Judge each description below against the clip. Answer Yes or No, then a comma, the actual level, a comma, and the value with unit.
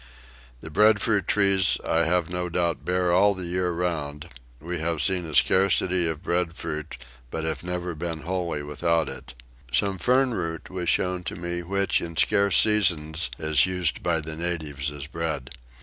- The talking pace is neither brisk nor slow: Yes, average, 165 wpm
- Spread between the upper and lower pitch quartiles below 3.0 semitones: Yes, narrow, 2.6 semitones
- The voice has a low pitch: Yes, very low, 85 Hz